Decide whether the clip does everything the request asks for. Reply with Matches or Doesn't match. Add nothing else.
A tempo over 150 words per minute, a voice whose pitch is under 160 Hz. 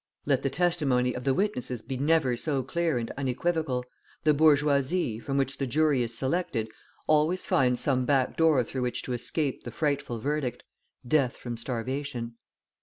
Matches